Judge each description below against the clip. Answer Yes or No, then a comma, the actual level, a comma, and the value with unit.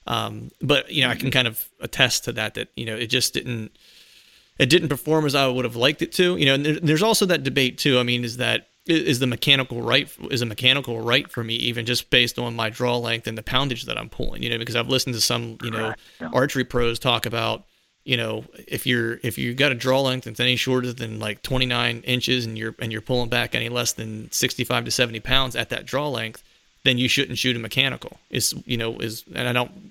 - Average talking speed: No, fast, 245 wpm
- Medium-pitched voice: No, low, 125 Hz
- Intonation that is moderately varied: No, narrow, 2.2 semitones